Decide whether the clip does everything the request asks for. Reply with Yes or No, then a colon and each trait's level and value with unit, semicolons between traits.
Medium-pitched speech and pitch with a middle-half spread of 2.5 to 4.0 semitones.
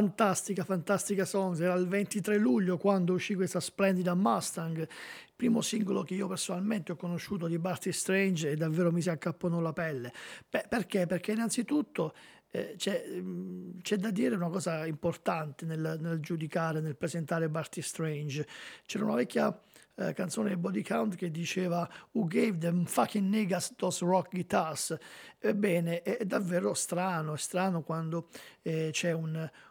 Yes: medium, 180 Hz; average, 2.8 semitones